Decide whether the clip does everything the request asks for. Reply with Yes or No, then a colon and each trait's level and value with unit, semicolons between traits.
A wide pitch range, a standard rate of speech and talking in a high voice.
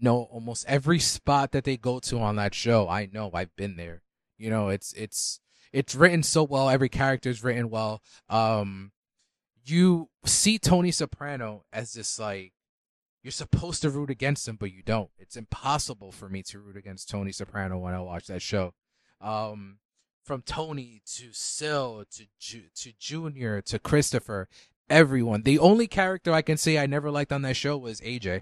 No: wide, 5.9 semitones; average, 180 wpm; low, 120 Hz